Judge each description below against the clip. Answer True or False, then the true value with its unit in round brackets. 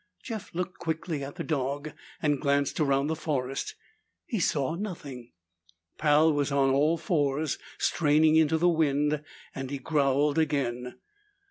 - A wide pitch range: False (2.5 semitones)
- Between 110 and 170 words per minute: True (140 wpm)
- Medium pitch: True (150 Hz)